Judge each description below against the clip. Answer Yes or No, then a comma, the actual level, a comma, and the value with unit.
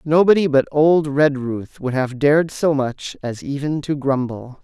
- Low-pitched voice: No, medium, 145 Hz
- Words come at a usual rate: Yes, average, 170 wpm